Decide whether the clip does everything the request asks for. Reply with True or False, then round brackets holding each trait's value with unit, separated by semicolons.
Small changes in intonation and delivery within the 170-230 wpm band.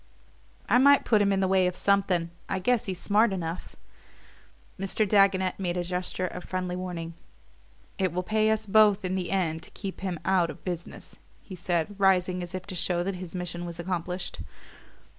True (1.8 semitones; 190 wpm)